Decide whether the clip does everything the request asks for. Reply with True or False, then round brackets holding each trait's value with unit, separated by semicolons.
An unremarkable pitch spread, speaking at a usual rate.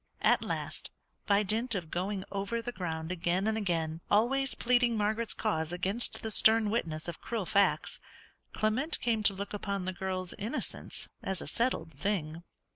True (4.1 semitones; 165 wpm)